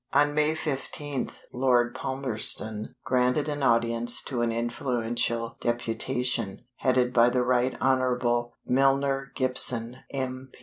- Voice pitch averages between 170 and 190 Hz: No, low, 125 Hz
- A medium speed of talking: No, slow, 115 wpm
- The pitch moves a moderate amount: No, narrow, 2.1 semitones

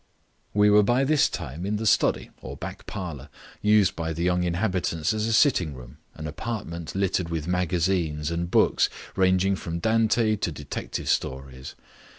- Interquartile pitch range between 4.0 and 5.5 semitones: Yes, average, 4.3 semitones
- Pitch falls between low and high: No, very low, 90 Hz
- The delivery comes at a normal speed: Yes, average, 160 wpm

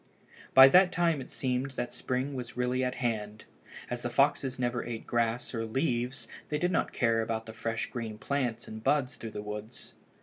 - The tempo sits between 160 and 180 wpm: No, average, 195 wpm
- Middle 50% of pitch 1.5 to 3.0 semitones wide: Yes, average, 2.7 semitones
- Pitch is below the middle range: Yes, low, 125 Hz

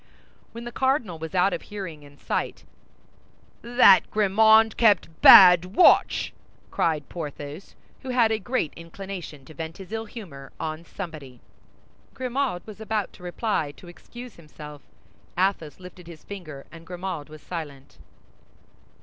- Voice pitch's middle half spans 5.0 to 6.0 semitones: Yes, wide, 5.6 semitones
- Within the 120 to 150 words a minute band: Yes, average, 140 wpm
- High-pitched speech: No, medium, 180 Hz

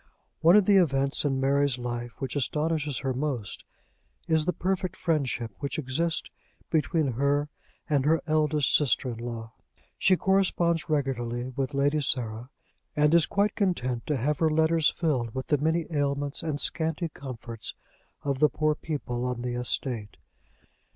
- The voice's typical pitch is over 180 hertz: No, medium, 145 Hz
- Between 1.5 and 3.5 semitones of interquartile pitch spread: No, average, 3.9 semitones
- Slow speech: No, average, 155 wpm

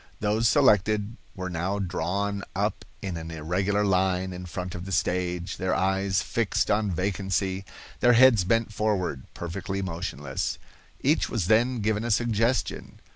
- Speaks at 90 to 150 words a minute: Yes, average, 145 wpm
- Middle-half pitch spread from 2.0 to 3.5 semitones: Yes, average, 2.9 semitones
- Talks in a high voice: No, very low, 95 Hz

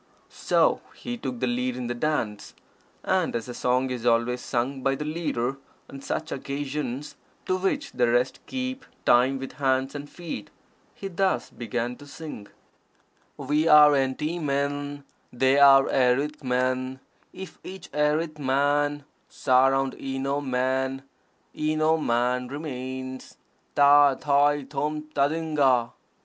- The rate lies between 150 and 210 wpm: No, slow, 135 wpm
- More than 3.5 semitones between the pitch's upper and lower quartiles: No, average, 2.8 semitones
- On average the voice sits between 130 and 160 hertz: Yes, low, 135 Hz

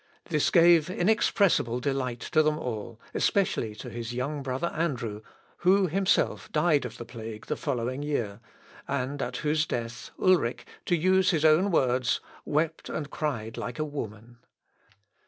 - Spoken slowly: No, average, 150 wpm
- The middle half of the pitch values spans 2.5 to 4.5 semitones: No, average, 5.3 semitones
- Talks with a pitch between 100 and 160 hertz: Yes, medium, 140 Hz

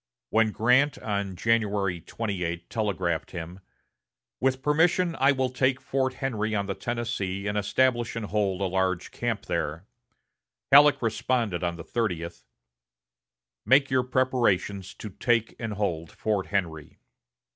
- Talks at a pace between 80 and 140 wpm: Yes, slow, 135 wpm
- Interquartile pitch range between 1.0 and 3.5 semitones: No, average, 5.3 semitones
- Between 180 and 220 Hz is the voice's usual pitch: No, low, 110 Hz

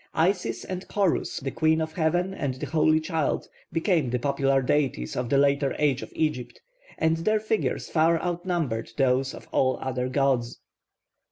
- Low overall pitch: No, medium, 150 Hz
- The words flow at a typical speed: Yes, average, 165 wpm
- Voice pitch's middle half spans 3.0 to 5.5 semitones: Yes, average, 4.0 semitones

